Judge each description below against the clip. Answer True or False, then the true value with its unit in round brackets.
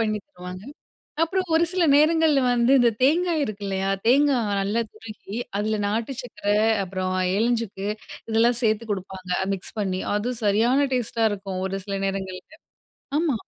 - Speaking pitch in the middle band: False (220 Hz)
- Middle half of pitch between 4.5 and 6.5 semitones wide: True (5.2 semitones)